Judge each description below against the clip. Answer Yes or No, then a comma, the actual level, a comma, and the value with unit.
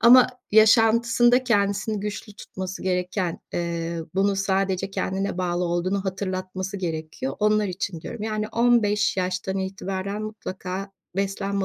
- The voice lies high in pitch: Yes, high, 195 Hz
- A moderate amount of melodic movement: No, narrow, 2.3 semitones